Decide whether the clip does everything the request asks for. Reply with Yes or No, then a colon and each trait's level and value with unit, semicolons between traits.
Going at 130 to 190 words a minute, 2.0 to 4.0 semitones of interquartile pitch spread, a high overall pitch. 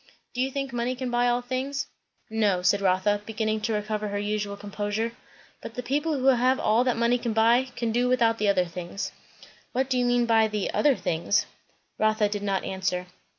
No: average, 200 wpm; average, 3.2 semitones; high, 225 Hz